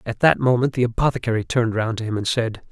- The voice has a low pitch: Yes, low, 115 Hz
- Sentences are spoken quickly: Yes, fast, 245 wpm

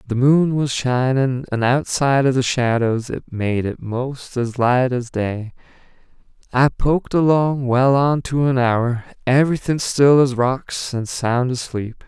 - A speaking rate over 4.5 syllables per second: No, 4.0 syllables/s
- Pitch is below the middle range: Yes, low, 130 Hz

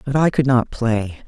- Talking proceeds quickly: Yes, fast, 235 wpm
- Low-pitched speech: Yes, low, 125 Hz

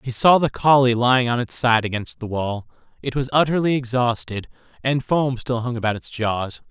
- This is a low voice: Yes, low, 125 Hz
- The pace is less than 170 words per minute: No, average, 195 wpm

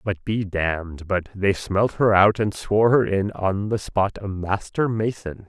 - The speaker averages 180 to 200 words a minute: Yes, average, 195 wpm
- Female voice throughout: No, male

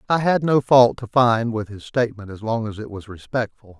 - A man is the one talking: Yes, male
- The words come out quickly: Yes, fast, 235 wpm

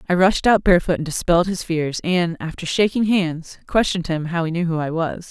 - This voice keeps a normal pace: No, fast, 225 wpm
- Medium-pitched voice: Yes, medium, 175 Hz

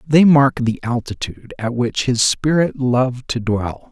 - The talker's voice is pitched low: Yes, low, 130 Hz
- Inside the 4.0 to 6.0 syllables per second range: Yes, 4.3 syllables/s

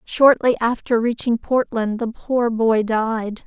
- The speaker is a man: No, female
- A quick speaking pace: No, average, 140 wpm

